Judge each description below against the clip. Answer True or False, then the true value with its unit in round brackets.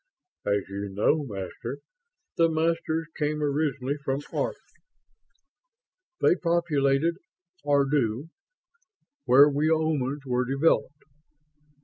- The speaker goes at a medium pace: False (90 wpm)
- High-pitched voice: False (145 Hz)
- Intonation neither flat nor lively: True (3.5 semitones)